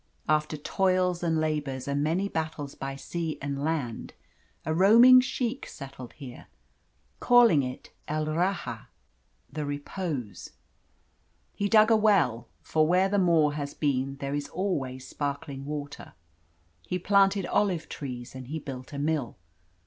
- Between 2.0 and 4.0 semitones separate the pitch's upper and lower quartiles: No, average, 4.9 semitones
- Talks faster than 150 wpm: No, average, 140 wpm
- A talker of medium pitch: Yes, medium, 155 Hz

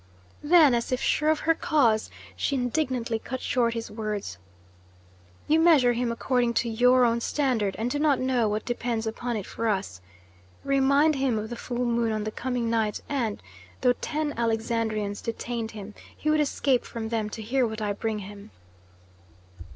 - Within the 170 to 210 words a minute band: Yes, average, 175 wpm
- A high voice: Yes, high, 235 Hz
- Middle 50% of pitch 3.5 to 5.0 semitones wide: No, average, 3.0 semitones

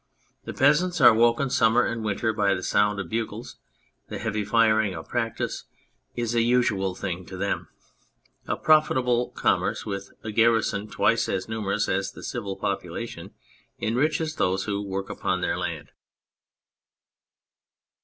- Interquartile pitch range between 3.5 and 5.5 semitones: No, average, 3.1 semitones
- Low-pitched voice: Yes, low, 110 Hz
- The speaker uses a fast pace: No, average, 145 wpm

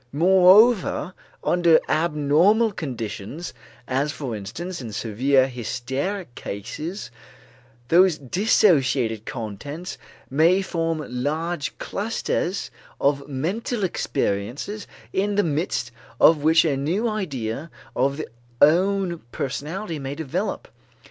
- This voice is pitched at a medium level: Yes, medium, 155 Hz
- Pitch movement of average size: No, wide, 5.7 semitones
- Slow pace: Yes, slow, 100 wpm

